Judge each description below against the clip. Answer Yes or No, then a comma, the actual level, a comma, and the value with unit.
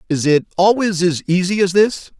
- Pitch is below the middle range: No, medium, 185 Hz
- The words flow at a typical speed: Yes, average, 190 wpm